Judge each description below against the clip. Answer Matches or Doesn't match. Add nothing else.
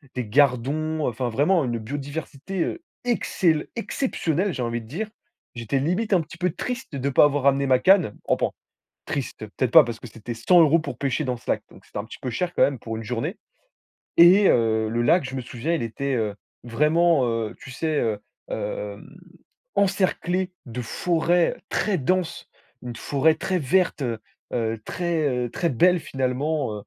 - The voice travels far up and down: Matches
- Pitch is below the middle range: Doesn't match